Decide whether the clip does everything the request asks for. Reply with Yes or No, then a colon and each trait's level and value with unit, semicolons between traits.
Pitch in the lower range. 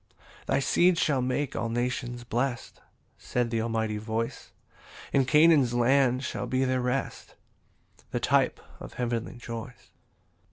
Yes: low, 125 Hz